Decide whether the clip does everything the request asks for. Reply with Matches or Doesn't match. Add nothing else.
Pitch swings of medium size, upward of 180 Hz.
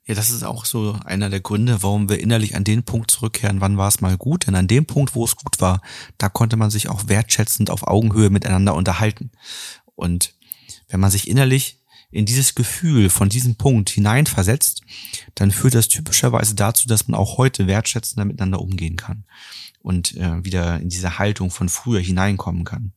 Doesn't match